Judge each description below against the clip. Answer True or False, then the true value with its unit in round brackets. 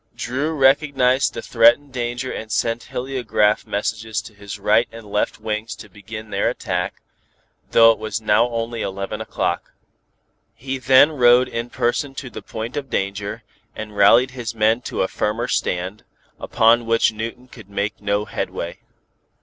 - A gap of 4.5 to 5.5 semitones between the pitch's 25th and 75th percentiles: False (2.9 semitones)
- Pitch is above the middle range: False (115 Hz)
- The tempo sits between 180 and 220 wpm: False (160 wpm)